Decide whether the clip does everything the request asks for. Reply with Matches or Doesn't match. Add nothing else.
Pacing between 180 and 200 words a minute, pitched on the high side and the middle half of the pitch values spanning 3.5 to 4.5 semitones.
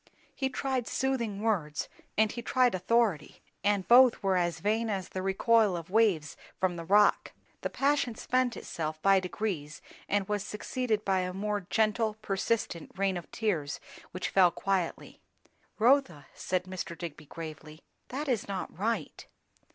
Doesn't match